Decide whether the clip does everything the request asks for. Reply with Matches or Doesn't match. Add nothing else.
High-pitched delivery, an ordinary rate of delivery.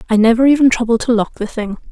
Doesn't match